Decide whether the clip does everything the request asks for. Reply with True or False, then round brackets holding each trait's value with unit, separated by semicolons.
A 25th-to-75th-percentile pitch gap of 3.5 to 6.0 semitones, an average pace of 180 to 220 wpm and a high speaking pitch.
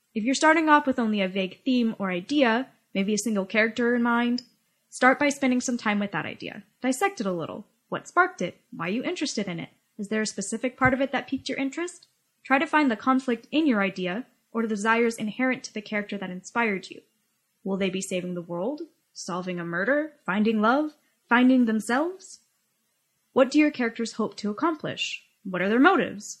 True (4.4 semitones; 205 wpm; 230 Hz)